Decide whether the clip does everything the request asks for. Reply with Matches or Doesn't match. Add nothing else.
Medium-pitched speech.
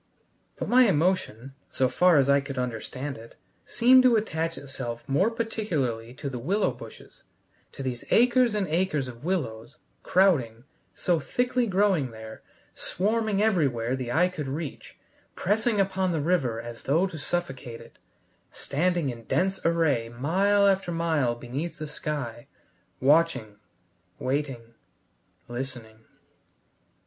Matches